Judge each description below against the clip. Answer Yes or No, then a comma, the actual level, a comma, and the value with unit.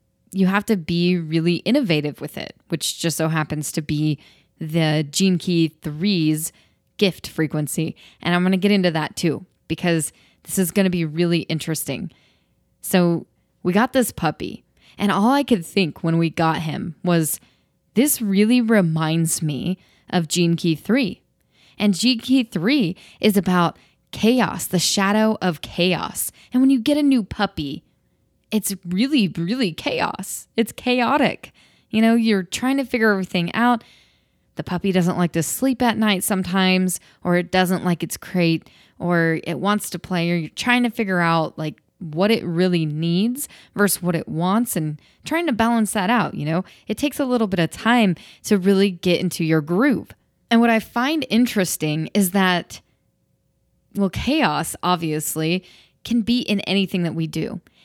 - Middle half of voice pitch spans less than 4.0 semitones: No, average, 4.7 semitones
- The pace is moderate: Yes, average, 170 wpm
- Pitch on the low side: No, medium, 180 Hz